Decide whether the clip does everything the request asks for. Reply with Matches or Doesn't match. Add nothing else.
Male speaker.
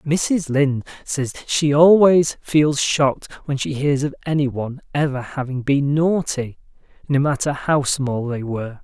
Matches